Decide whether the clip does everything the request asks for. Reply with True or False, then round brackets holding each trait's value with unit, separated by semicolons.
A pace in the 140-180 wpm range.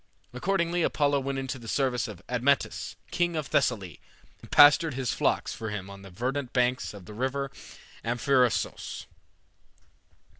True (145 wpm)